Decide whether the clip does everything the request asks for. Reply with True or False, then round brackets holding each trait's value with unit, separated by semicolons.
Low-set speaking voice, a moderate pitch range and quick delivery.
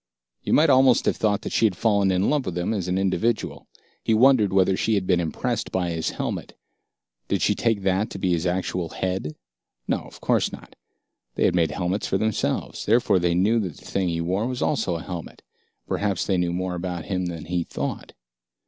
True (95 Hz; 3.4 semitones; 210 wpm)